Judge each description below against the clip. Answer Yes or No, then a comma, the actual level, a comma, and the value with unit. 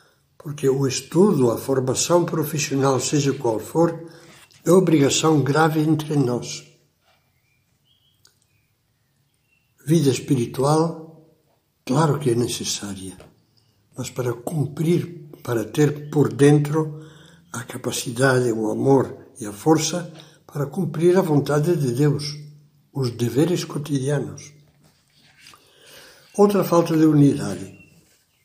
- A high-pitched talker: No, medium, 145 Hz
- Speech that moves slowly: Yes, slow, 100 wpm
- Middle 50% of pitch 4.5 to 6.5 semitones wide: No, average, 3.9 semitones